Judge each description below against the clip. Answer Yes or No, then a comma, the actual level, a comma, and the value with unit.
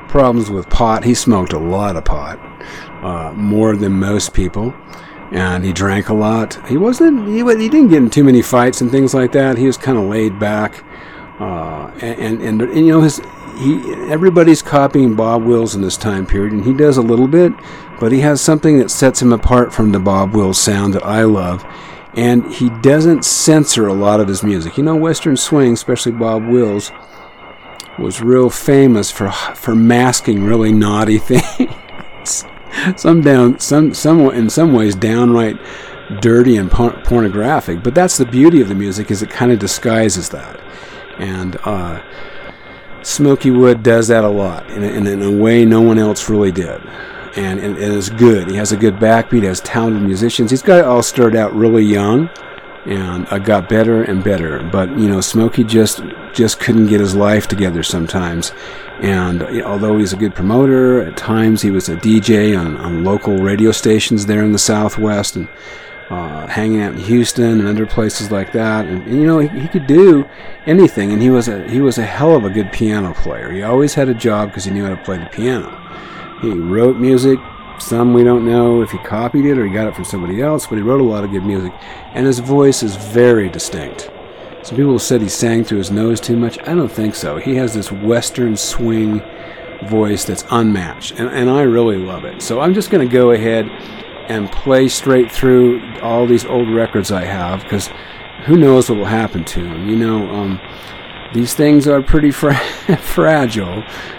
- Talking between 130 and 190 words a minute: No, average, 200 wpm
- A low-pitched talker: Yes, low, 115 Hz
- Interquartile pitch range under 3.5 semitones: No, average, 4.0 semitones